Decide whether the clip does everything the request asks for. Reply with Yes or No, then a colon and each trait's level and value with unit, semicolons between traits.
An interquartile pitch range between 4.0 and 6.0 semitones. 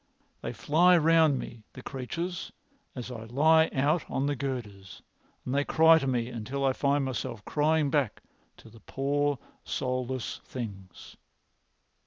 No: average, 3.5 semitones